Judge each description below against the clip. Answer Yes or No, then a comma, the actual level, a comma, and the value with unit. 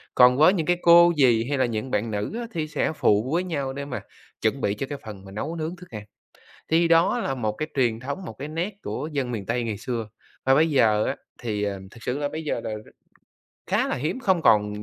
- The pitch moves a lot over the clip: Yes, wide, 6.3 semitones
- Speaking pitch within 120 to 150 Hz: Yes, low, 135 Hz